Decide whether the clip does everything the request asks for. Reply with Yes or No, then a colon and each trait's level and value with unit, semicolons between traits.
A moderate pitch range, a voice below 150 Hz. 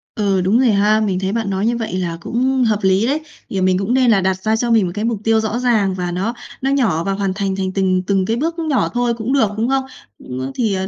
No: average, 3.9 semitones; high, 210 Hz